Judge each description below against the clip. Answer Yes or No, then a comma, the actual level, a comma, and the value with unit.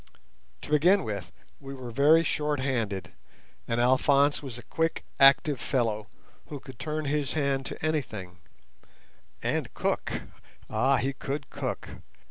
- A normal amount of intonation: Yes, average, 3.9 semitones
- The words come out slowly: Yes, slow, 130 wpm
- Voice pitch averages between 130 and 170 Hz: Yes, low, 135 Hz